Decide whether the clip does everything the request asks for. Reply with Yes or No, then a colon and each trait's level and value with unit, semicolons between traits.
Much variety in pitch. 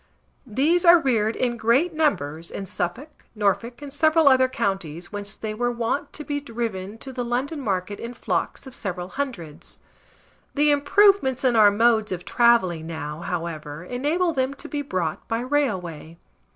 Yes: wide, 7.2 semitones